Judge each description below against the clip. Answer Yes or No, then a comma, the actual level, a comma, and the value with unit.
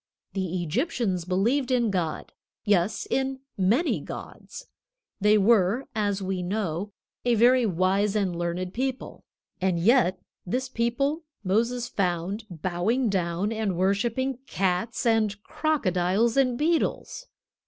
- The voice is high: Yes, high, 210 Hz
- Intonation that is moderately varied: Yes, average, 4.8 semitones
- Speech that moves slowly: Yes, slow, 120 wpm